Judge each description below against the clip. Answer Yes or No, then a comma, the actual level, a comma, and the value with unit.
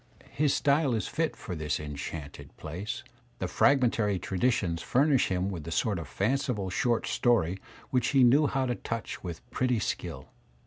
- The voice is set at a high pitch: No, low, 110 Hz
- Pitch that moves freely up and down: Yes, wide, 7.0 semitones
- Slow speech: No, average, 170 wpm